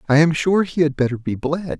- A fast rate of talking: Yes, fast, 265 wpm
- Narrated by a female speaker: No, male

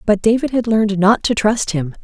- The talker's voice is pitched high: Yes, high, 210 Hz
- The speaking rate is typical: No, fast, 235 wpm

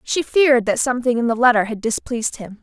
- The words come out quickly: Yes, fast, 230 wpm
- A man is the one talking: No, female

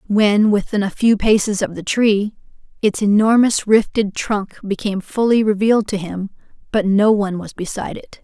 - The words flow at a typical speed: Yes, average, 165 wpm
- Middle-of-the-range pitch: No, high, 205 Hz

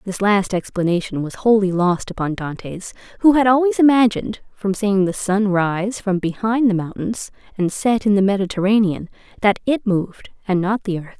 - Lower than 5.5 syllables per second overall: Yes, 5.0 syllables/s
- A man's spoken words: No, female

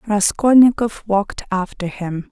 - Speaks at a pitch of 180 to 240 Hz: Yes, high, 205 Hz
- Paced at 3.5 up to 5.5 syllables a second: Yes, 4.4 syllables/s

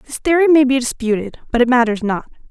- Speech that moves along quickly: Yes, fast, 215 wpm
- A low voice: No, very high, 250 Hz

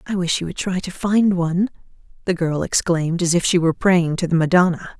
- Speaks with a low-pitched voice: No, medium, 175 Hz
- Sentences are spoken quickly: Yes, fast, 230 wpm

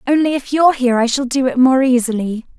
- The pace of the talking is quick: Yes, fast, 230 wpm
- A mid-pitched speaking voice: No, very high, 260 Hz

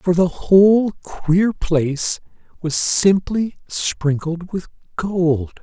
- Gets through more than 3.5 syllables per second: No, 2.9 syllables/s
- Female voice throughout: No, male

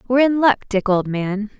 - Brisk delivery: Yes, fast, 225 wpm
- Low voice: No, high, 225 Hz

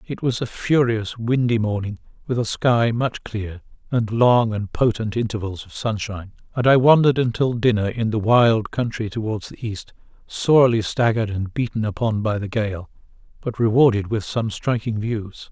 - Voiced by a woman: No, male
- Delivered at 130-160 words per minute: No, average, 170 wpm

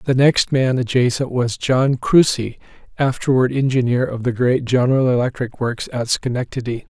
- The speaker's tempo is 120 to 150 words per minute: Yes, average, 145 wpm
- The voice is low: Yes, low, 125 Hz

